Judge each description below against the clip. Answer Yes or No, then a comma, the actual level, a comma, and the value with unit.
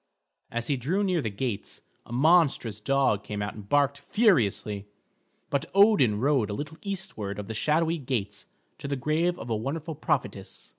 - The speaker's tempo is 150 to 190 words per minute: Yes, average, 170 wpm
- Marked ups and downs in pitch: Yes, wide, 6.9 semitones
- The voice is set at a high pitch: No, low, 135 Hz